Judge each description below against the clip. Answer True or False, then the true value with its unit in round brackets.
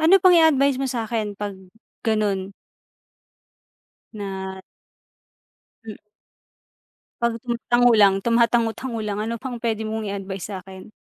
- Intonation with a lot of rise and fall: False (3.0 semitones)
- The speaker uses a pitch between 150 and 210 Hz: False (220 Hz)